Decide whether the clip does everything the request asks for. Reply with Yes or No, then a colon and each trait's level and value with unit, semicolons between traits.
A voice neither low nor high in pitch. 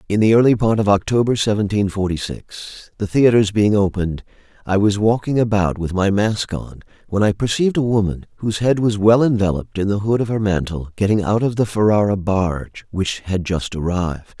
No: low, 100 Hz